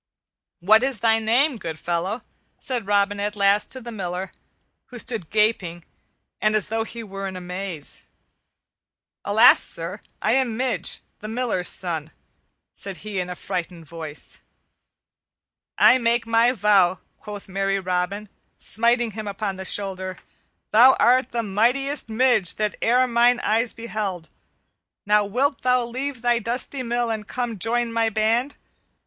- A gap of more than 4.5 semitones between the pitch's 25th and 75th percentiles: No, average, 3.7 semitones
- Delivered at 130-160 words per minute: Yes, average, 150 wpm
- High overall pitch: Yes, high, 215 Hz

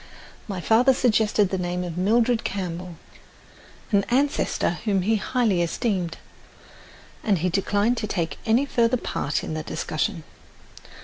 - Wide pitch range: No, average, 4.5 semitones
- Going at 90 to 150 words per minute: Yes, slow, 135 wpm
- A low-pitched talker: No, high, 200 Hz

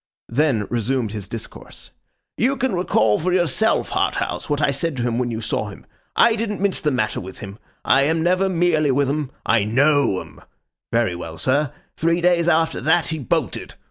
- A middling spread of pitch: No, wide, 6.7 semitones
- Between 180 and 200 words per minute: Yes, average, 190 wpm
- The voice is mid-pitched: Yes, medium, 145 Hz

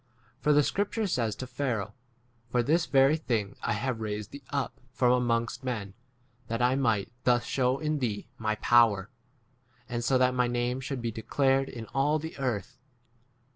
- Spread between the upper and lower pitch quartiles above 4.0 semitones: No, average, 3.0 semitones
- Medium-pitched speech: No, low, 125 Hz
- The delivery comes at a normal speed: Yes, average, 175 wpm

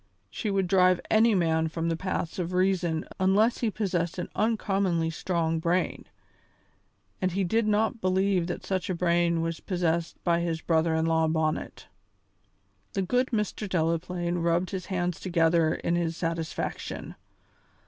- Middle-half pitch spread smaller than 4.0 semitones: Yes, narrow, 2.4 semitones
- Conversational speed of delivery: Yes, average, 150 wpm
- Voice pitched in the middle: Yes, medium, 175 Hz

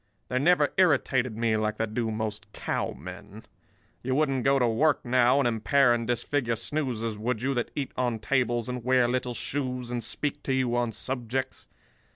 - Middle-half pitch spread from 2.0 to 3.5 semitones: Yes, average, 2.7 semitones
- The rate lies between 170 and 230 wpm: Yes, average, 180 wpm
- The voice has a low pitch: Yes, low, 120 Hz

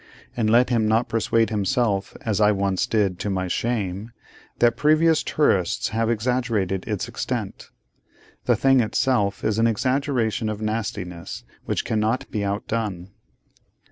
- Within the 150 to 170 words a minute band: No, average, 140 wpm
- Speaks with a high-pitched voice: No, low, 110 Hz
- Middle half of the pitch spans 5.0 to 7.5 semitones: No, average, 3.1 semitones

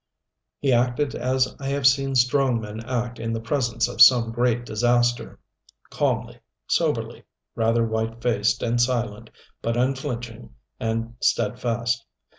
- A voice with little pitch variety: Yes, narrow, 1.9 semitones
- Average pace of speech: No, slow, 130 wpm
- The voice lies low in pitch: Yes, low, 120 Hz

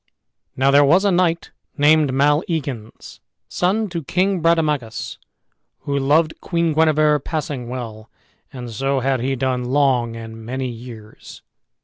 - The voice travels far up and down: No, average, 4.2 semitones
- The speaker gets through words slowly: Yes, slow, 130 wpm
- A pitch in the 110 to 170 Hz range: Yes, medium, 140 Hz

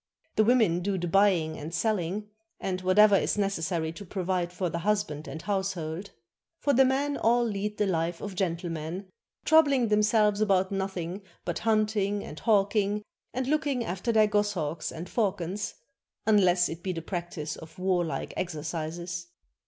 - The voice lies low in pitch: No, high, 190 Hz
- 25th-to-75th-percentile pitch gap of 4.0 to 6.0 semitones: No, average, 3.5 semitones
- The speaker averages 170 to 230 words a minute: No, average, 155 wpm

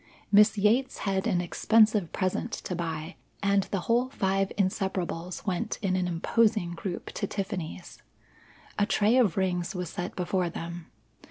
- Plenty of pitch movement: No, average, 3.0 semitones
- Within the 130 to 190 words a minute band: Yes, average, 150 wpm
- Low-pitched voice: No, high, 190 Hz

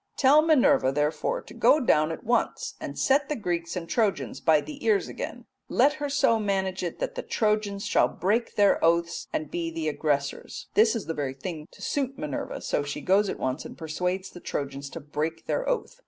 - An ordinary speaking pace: No, fast, 210 wpm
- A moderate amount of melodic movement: No, wide, 7.2 semitones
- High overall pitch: No, medium, 180 Hz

